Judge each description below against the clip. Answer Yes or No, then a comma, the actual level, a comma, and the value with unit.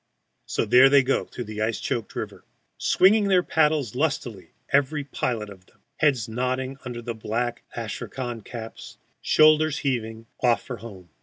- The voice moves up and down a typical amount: Yes, average, 4.0 semitones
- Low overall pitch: Yes, low, 125 Hz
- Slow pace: No, average, 150 wpm